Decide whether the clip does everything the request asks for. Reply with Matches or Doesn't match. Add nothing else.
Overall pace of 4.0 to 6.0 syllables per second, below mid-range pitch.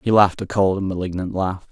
Doesn't match